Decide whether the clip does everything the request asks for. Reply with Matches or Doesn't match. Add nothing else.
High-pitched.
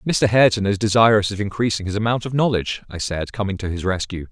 Doesn't match